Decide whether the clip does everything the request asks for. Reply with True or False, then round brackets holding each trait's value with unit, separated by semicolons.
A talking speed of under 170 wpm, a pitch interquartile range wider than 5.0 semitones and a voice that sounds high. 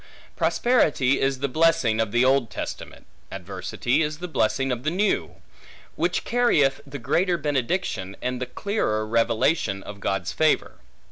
False (145 wpm; 5.6 semitones; 135 Hz)